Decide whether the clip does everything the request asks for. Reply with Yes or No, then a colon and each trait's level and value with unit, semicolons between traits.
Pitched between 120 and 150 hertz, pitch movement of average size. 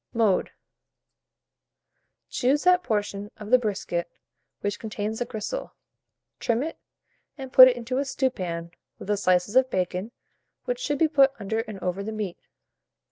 No: high, 220 Hz; average, 4.7 semitones